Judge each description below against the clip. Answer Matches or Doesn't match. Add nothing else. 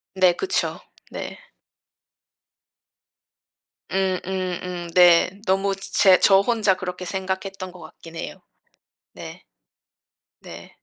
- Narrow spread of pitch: Matches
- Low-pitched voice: Doesn't match